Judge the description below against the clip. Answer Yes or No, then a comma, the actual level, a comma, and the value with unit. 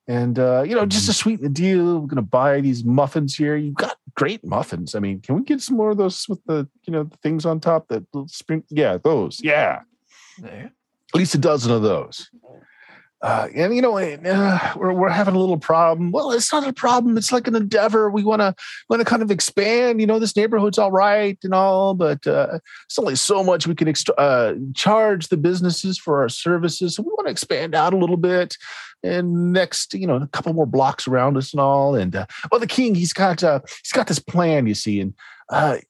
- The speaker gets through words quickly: Yes, fast, 225 wpm